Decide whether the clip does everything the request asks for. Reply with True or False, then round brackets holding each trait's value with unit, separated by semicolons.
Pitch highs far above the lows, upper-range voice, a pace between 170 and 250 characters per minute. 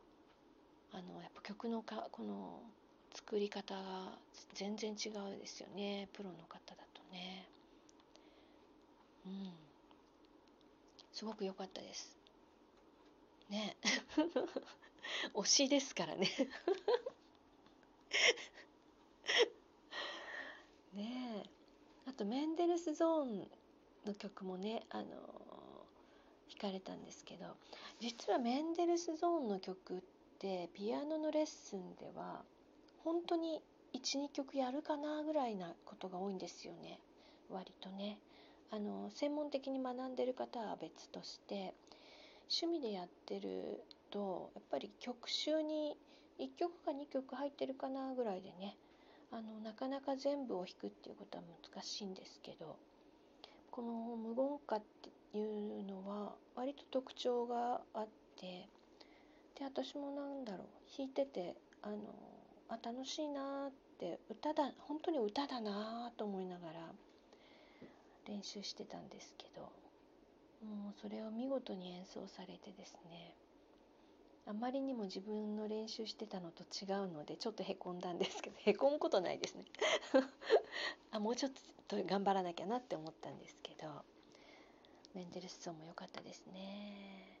True (6.6 semitones; 230 Hz; 240 characters per minute)